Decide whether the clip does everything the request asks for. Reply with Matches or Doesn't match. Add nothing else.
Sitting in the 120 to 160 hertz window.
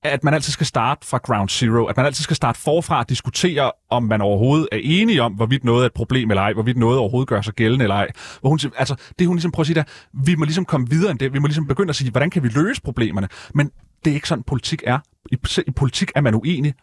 Matches